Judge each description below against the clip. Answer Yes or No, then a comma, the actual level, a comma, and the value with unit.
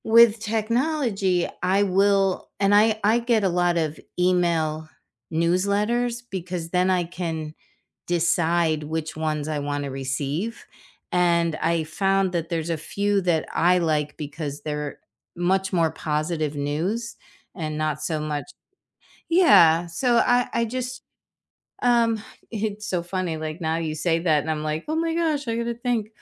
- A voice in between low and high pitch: Yes, medium, 175 Hz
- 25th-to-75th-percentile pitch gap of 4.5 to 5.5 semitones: Yes, average, 5.2 semitones